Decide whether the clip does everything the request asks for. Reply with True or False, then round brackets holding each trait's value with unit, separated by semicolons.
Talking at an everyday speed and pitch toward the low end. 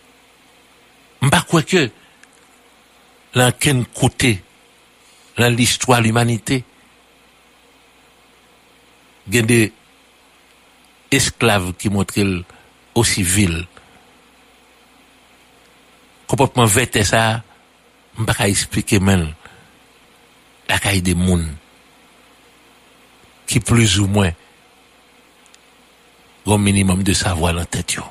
False (80 wpm; 120 Hz)